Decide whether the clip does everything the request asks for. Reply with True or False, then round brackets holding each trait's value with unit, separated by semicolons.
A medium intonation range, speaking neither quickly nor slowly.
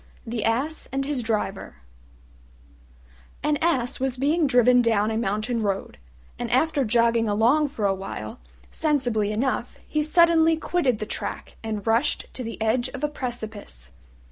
True (4.7 semitones; 150 wpm)